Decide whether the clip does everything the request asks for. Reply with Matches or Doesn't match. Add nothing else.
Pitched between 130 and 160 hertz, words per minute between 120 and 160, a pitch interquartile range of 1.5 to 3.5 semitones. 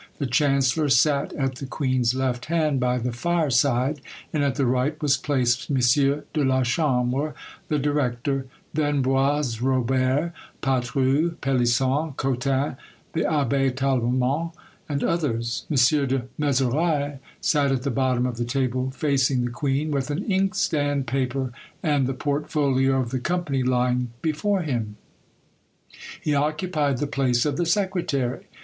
Matches